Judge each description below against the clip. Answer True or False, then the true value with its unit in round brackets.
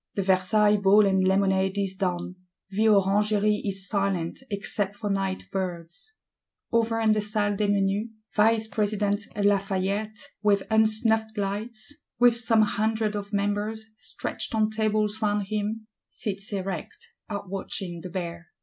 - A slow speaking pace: True (130 wpm)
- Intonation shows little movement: True (1.8 semitones)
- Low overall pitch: False (205 Hz)